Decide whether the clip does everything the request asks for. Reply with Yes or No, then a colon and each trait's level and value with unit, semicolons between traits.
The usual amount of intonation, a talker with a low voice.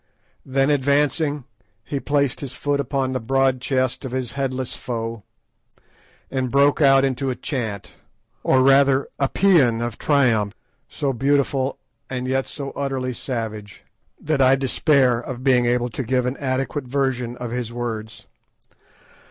No: narrow, 2.2 semitones; low, 130 Hz